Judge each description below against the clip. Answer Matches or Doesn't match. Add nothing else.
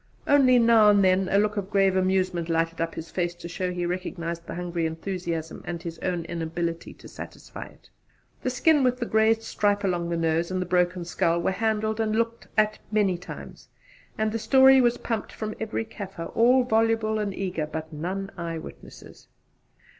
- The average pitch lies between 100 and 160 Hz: Doesn't match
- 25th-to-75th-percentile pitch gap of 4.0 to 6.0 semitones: Matches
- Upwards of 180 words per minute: Matches